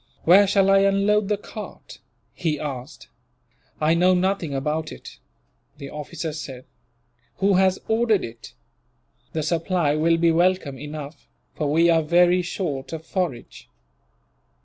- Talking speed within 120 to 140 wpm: Yes, slow, 135 wpm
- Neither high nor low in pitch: Yes, medium, 165 Hz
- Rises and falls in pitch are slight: No, average, 4.0 semitones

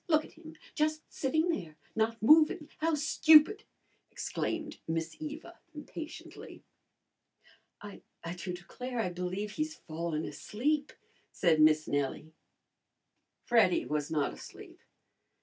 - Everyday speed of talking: No, slow, 115 wpm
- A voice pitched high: Yes, high, 240 Hz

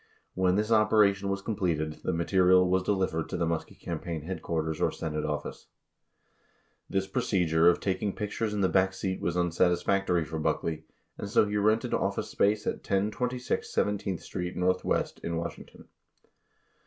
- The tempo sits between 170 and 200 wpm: No, average, 155 wpm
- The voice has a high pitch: No, very low, 95 Hz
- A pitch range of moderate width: Yes, average, 3.1 semitones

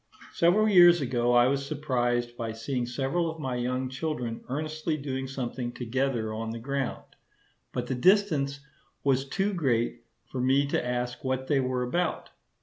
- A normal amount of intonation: Yes, average, 3.3 semitones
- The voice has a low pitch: Yes, low, 130 Hz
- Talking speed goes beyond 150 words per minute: Yes, average, 160 wpm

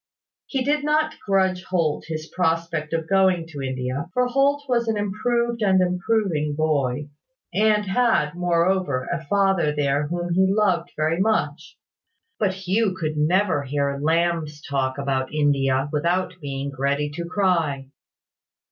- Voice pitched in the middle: Yes, medium, 170 Hz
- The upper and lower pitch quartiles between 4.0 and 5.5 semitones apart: Yes, average, 4.7 semitones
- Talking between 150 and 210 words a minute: No, average, 140 wpm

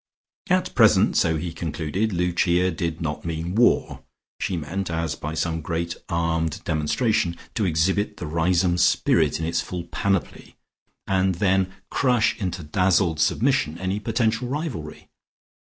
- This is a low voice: Yes, very low, 85 Hz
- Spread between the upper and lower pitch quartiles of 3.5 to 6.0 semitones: No, average, 3.0 semitones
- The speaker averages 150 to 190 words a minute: No, average, 140 wpm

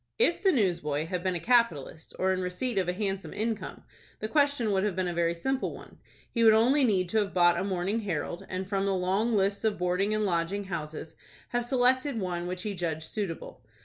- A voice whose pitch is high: Yes, high, 195 Hz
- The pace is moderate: No, fast, 215 wpm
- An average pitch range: Yes, average, 3.9 semitones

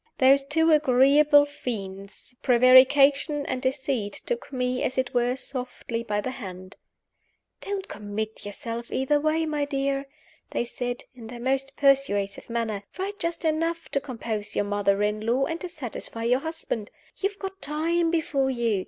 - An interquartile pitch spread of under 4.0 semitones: No, average, 4.4 semitones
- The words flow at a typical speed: Yes, average, 160 wpm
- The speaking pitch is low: No, very high, 260 Hz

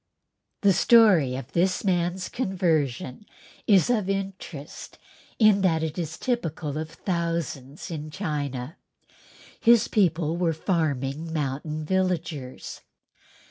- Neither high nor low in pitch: Yes, medium, 165 Hz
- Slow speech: Yes, slow, 105 wpm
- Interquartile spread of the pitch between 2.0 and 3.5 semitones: No, average, 4.1 semitones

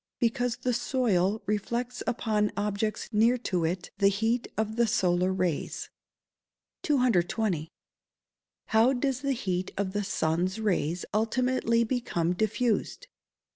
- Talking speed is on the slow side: Yes, slow, 125 wpm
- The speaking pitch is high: Yes, high, 220 Hz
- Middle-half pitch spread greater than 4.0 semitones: Yes, average, 4.4 semitones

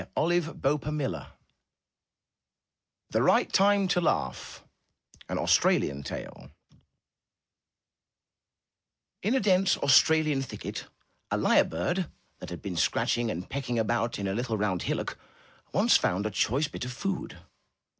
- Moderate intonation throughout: No, wide, 8.4 semitones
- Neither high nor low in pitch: No, low, 130 Hz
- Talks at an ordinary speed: No, slow, 130 wpm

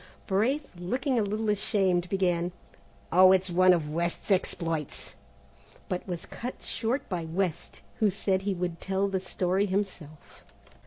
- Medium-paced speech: Yes, average, 145 wpm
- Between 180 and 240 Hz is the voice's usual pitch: Yes, medium, 185 Hz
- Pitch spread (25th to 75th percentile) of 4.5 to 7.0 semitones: No, narrow, 2.5 semitones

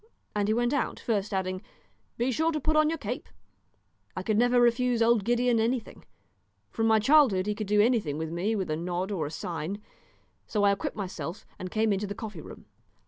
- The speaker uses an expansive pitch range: No, average, 4.1 semitones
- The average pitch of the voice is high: Yes, high, 215 Hz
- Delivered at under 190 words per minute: No, fast, 205 wpm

